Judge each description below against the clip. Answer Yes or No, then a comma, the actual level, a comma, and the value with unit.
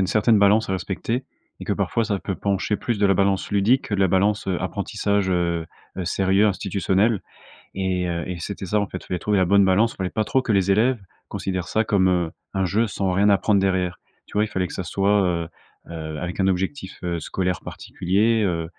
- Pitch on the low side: Yes, very low, 95 Hz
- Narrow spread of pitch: Yes, narrow, 2.2 semitones